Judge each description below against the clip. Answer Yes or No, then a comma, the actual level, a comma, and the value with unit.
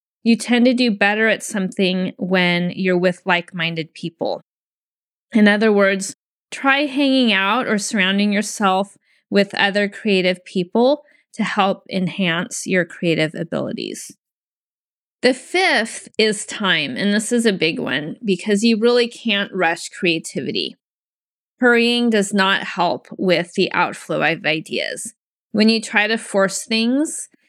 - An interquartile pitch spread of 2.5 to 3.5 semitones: No, average, 4.0 semitones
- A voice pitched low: No, high, 205 Hz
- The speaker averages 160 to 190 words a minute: No, average, 140 wpm